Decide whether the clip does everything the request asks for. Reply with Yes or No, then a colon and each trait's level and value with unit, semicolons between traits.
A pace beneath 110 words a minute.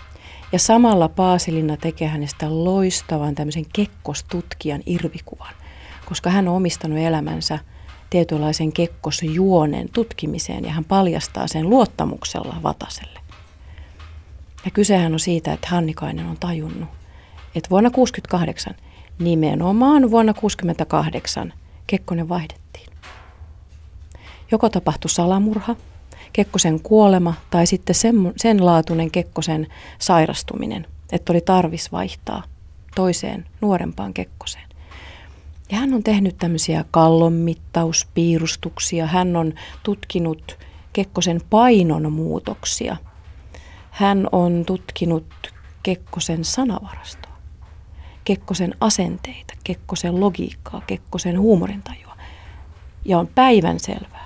Yes: slow, 95 wpm